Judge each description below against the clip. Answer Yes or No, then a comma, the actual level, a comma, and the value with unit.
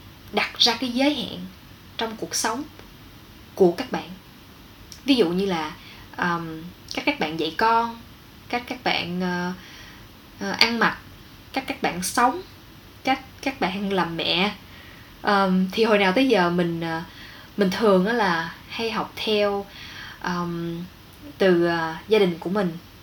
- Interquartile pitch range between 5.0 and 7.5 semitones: Yes, wide, 5.5 semitones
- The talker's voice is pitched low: No, medium, 185 Hz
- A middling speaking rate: No, slow, 150 wpm